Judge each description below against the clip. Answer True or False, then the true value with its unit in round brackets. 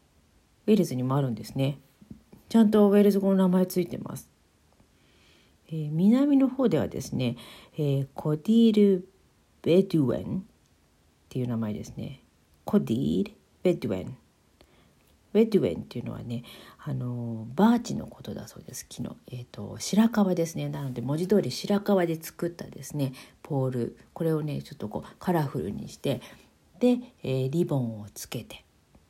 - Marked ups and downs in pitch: True (8.2 semitones)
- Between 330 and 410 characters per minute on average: False (310 characters per minute)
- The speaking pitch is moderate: True (155 Hz)